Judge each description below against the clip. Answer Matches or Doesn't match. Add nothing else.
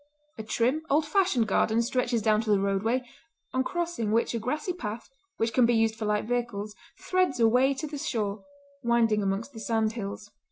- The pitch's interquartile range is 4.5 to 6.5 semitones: Doesn't match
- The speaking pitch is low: Doesn't match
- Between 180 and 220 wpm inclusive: Matches